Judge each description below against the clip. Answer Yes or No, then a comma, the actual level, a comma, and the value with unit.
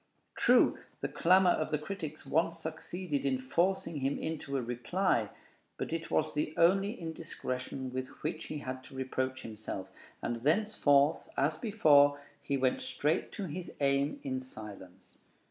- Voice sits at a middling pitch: Yes, medium, 145 Hz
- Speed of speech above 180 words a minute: No, average, 150 wpm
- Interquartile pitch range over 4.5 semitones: No, average, 4.2 semitones